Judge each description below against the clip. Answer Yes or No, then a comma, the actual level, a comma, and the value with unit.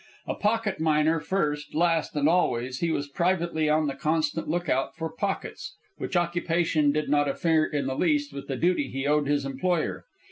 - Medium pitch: Yes, medium, 155 Hz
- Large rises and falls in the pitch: No, average, 3.0 semitones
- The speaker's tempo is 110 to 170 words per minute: No, average, 180 wpm